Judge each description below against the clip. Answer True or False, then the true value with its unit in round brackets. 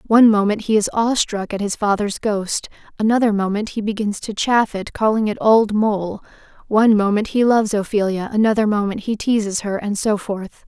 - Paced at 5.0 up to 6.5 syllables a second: True (5.3 syllables/s)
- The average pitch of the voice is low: False (210 Hz)